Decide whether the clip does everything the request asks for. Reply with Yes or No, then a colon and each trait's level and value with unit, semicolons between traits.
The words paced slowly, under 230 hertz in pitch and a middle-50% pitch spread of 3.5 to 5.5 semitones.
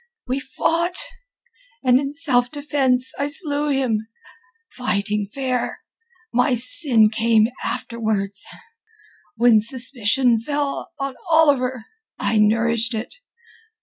No: slow, 95 wpm; very high, 250 Hz; average, 3.9 semitones